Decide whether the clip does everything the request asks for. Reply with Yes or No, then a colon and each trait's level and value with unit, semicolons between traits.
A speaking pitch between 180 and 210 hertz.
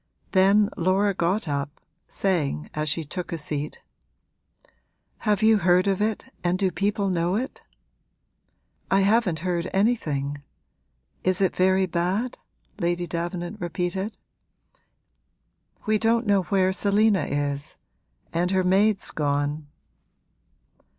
Yes: medium, 185 Hz